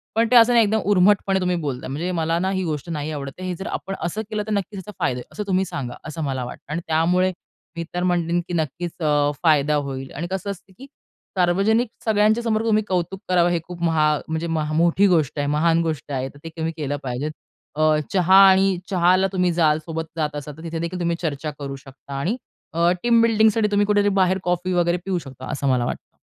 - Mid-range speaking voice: Yes, medium, 170 Hz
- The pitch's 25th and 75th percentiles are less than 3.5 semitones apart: No, average, 4.0 semitones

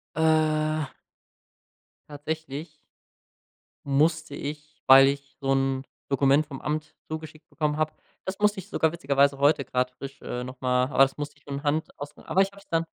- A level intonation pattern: Yes, narrow, 2.3 semitones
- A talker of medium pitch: Yes, medium, 150 Hz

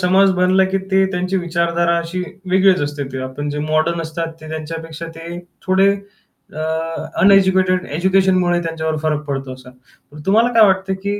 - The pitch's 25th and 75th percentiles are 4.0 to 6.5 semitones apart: No, average, 3.1 semitones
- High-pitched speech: No, medium, 175 Hz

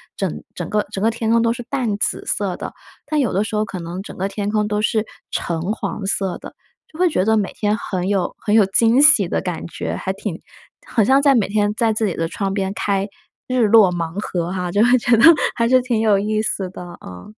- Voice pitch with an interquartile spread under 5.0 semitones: Yes, average, 3.0 semitones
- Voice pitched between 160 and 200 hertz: No, high, 210 Hz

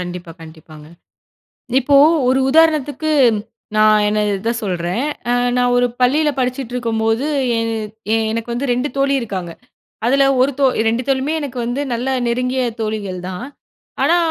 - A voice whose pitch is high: Yes, high, 245 Hz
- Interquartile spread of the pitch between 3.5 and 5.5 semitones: Yes, average, 4.1 semitones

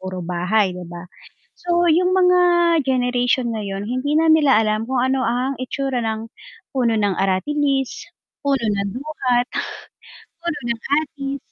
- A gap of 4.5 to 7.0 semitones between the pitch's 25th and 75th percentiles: Yes, average, 4.8 semitones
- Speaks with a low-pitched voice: No, very high, 250 Hz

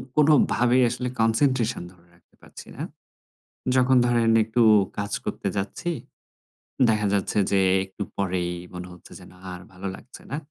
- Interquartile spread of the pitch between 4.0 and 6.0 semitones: Yes, average, 4.6 semitones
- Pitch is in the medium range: No, low, 110 Hz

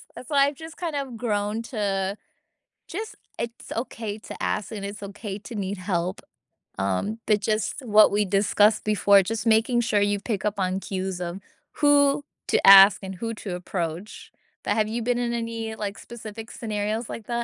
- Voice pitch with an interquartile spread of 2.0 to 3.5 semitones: Yes, average, 2.7 semitones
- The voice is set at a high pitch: Yes, high, 210 Hz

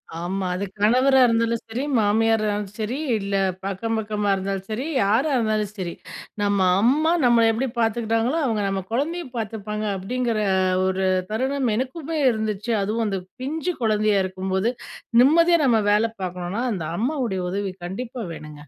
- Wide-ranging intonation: No, average, 3.8 semitones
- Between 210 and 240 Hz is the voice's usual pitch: Yes, high, 220 Hz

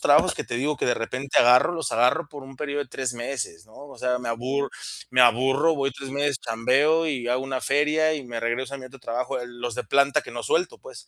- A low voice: Yes, low, 130 Hz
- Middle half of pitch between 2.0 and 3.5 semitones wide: Yes, average, 2.7 semitones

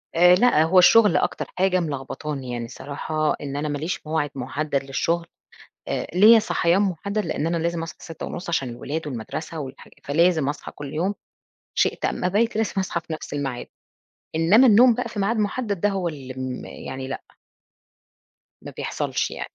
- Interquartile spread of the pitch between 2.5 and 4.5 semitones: No, average, 5.2 semitones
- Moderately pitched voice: Yes, medium, 165 Hz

